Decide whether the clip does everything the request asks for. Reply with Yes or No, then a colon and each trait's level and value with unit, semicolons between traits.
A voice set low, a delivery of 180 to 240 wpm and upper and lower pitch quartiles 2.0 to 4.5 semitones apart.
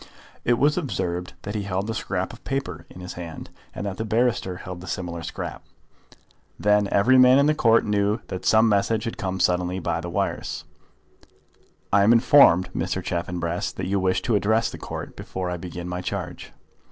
Yes: low, 100 Hz; average, 190 wpm; average, 4.0 semitones